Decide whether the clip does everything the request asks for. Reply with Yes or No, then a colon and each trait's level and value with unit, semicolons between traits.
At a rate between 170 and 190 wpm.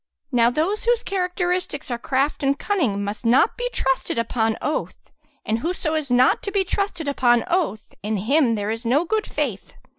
Yes: average, 180 wpm